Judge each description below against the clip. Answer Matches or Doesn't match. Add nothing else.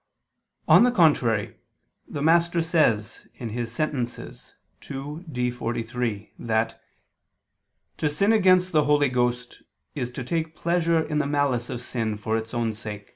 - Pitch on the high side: Doesn't match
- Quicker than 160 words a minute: Doesn't match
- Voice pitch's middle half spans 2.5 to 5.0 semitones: Doesn't match